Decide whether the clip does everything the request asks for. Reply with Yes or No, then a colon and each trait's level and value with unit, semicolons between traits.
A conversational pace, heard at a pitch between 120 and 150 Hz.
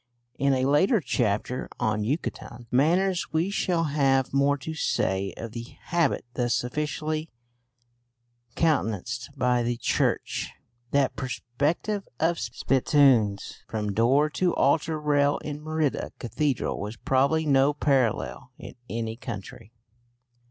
No: slow, 120 wpm; low, 135 Hz